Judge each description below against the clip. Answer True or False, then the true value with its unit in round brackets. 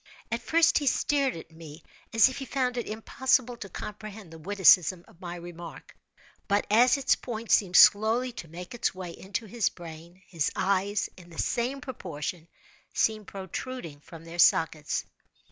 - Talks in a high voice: True (195 Hz)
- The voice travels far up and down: True (5.7 semitones)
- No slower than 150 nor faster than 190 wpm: True (165 wpm)